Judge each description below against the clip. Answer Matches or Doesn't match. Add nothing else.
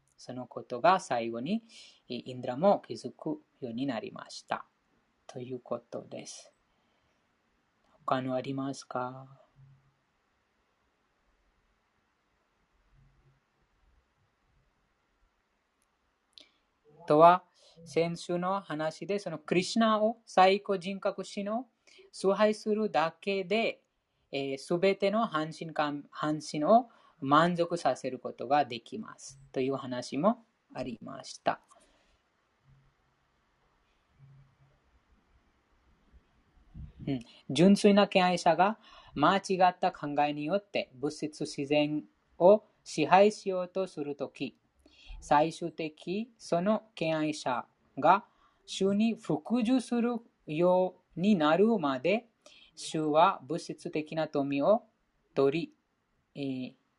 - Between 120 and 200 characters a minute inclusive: Matches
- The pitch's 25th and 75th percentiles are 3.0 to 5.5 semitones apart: Doesn't match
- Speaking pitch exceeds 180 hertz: Doesn't match